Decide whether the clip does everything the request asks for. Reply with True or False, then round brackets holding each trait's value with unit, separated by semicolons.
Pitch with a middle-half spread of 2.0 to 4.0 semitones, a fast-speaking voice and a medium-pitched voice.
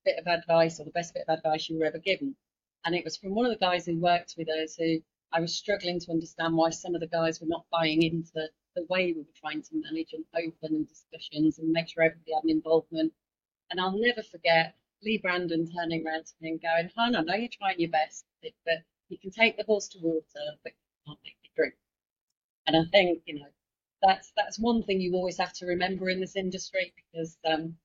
True (2.7 semitones; 235 wpm; 170 Hz)